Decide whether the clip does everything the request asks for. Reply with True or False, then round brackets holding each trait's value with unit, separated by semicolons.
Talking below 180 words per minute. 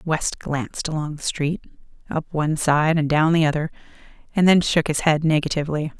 True (160 wpm)